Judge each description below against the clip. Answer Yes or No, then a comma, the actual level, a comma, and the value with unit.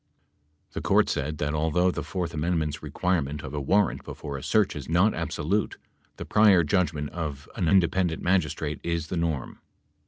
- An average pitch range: Yes, average, 3.6 semitones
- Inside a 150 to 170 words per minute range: Yes, average, 165 wpm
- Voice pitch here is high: No, very low, 85 Hz